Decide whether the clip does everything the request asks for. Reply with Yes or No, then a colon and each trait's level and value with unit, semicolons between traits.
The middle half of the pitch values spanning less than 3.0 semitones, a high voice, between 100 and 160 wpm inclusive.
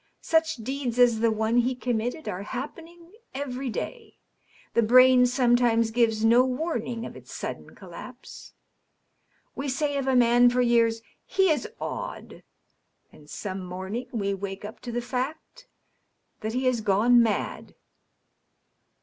Yes: narrow, 2.6 semitones; high, 245 Hz; average, 145 wpm